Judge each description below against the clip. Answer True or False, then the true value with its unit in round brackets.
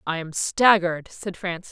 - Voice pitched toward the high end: False (180 Hz)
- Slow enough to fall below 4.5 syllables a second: False (5.0 syllables/s)